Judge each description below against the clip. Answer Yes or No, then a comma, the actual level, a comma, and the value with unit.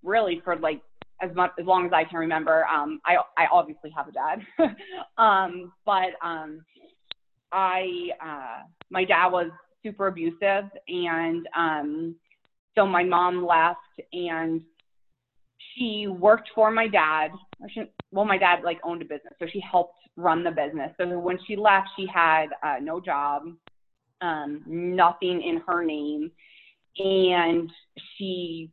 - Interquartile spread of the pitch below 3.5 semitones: Yes, average, 2.7 semitones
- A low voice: No, medium, 175 Hz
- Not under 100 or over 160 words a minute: Yes, average, 145 wpm